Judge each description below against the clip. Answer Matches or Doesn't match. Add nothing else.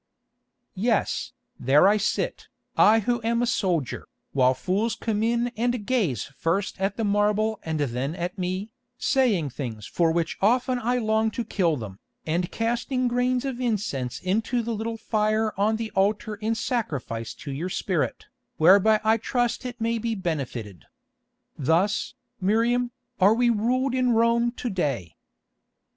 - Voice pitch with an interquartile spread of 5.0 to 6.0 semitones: Matches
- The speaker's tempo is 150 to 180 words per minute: Matches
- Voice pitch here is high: Matches